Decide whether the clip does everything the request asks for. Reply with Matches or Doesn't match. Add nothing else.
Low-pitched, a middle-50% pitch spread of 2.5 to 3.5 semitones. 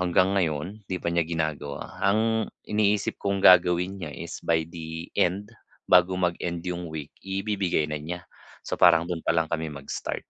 Matches